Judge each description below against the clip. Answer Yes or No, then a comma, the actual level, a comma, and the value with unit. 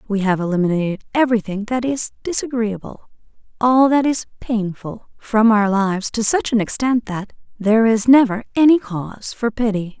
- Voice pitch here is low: No, high, 220 Hz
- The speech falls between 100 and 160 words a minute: Yes, average, 155 wpm